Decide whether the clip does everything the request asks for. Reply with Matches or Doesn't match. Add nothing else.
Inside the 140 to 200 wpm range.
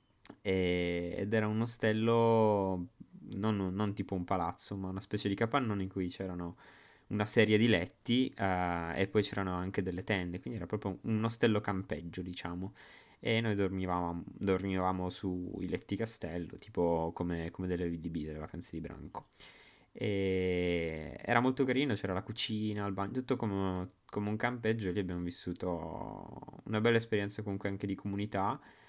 Matches